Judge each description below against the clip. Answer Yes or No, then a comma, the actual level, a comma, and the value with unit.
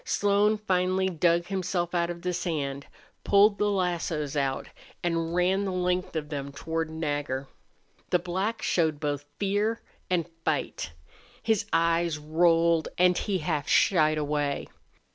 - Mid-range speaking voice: Yes, medium, 170 Hz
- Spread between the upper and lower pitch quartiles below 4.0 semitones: Yes, average, 3.3 semitones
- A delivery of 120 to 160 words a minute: Yes, average, 140 wpm